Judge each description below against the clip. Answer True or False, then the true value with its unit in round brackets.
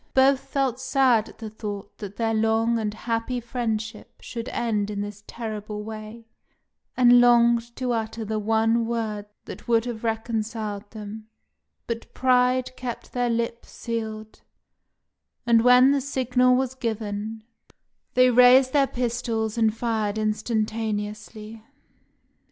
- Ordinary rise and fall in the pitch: False (2.1 semitones)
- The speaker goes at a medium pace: False (130 wpm)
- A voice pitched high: True (225 Hz)